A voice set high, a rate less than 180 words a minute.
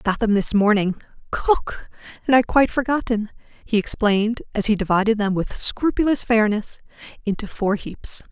Yes: high, 220 Hz; average, 160 wpm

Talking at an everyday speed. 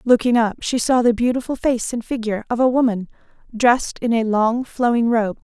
Yes: average, 195 wpm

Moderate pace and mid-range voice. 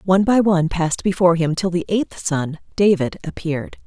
Yes: average, 185 wpm; medium, 175 Hz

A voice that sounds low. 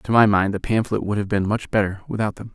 Yes: low, 105 Hz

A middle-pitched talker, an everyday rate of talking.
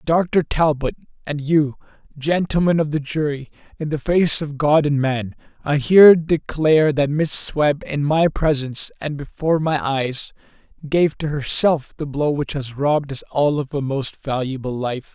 Yes: medium, 145 Hz; average, 170 wpm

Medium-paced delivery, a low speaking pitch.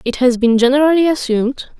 No: average, 170 wpm; very high, 260 Hz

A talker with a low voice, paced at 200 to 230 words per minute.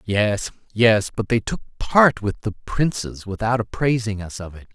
No: low, 110 Hz; average, 175 wpm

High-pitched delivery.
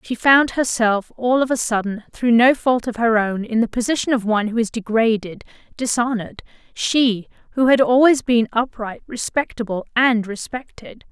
Yes: high, 235 Hz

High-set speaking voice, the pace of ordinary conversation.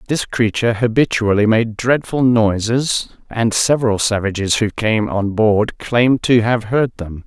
No: low, 115 Hz; average, 150 wpm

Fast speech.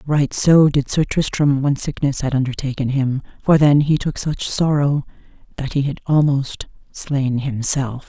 No: average, 165 wpm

